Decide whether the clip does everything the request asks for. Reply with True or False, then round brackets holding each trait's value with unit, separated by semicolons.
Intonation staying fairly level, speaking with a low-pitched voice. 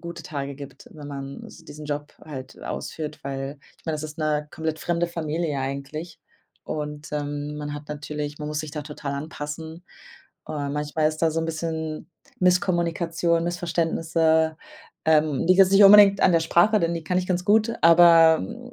False (2.3 semitones; 160 Hz)